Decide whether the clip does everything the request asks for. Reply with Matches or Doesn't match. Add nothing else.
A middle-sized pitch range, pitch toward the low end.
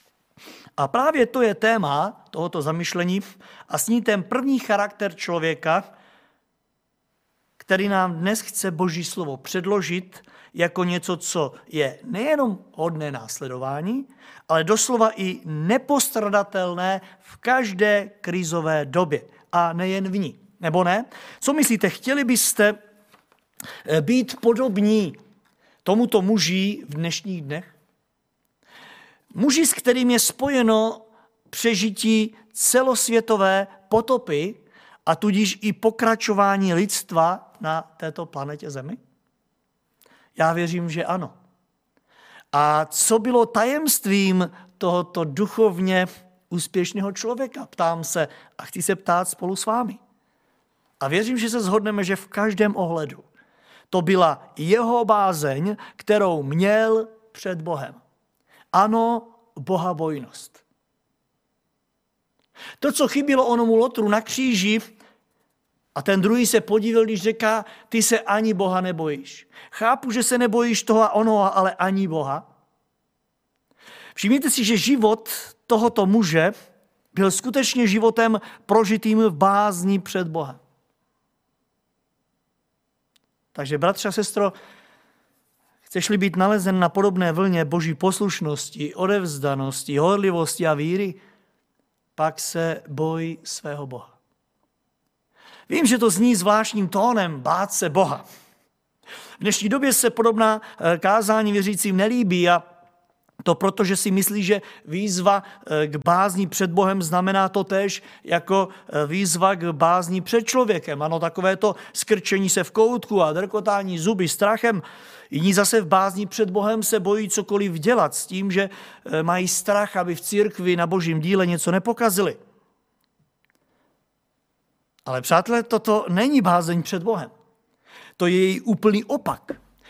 Doesn't match